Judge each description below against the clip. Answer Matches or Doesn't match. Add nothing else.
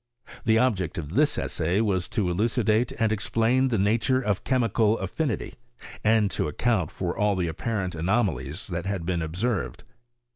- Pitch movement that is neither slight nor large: Matches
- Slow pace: Doesn't match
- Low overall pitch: Matches